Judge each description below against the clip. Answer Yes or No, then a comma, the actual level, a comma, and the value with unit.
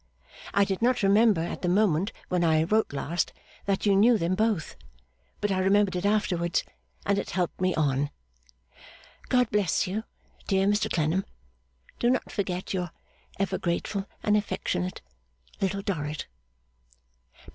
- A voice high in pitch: Yes, high, 195 Hz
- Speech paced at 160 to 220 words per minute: No, average, 145 wpm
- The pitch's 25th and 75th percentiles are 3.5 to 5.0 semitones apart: No, average, 2.9 semitones